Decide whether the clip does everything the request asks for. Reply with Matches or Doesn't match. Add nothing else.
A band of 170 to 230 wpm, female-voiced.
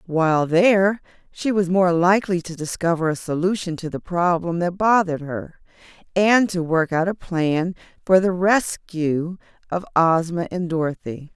Doesn't match